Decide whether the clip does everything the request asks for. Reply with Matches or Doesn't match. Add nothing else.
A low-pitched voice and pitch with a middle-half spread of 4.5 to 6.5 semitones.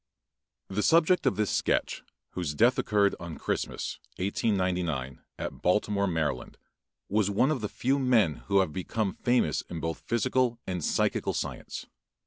Matches